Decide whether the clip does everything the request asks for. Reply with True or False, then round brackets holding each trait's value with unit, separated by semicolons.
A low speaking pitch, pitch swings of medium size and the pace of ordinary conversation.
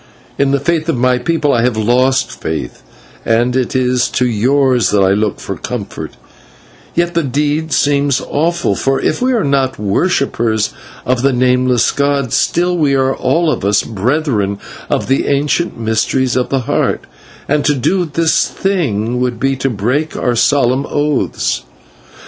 True (130 Hz; 3.4 semitones; 165 wpm)